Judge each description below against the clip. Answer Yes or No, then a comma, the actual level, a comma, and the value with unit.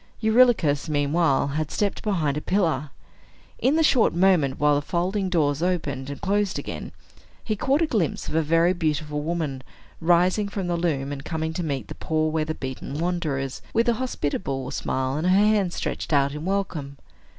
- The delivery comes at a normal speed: Yes, average, 180 wpm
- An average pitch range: Yes, average, 4.8 semitones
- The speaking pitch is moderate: Yes, medium, 160 Hz